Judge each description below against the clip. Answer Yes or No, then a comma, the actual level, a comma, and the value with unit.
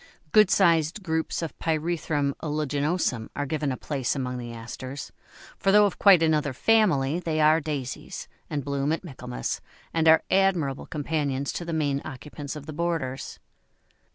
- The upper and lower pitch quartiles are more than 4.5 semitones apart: No, average, 3.1 semitones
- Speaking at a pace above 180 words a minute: No, average, 155 wpm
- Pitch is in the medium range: Yes, medium, 150 Hz